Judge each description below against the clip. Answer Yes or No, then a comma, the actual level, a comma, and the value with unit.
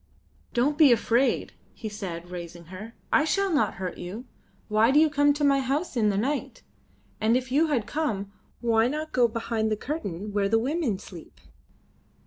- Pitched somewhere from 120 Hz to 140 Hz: No, high, 235 Hz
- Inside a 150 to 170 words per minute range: No, average, 185 wpm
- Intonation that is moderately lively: No, wide, 5.9 semitones